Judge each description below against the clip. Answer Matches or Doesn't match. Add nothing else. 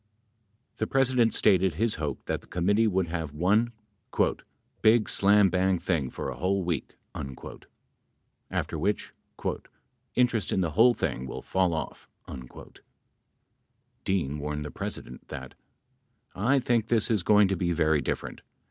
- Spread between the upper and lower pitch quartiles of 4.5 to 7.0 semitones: Matches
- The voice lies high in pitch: Doesn't match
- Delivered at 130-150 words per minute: Matches